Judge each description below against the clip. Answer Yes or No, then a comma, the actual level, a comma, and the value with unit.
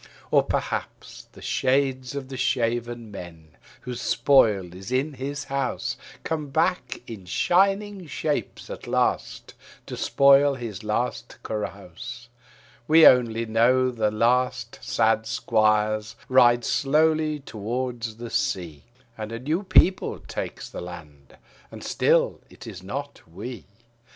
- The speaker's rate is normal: No, slow, 125 wpm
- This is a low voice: Yes, low, 120 Hz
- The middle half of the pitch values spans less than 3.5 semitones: No, average, 4.3 semitones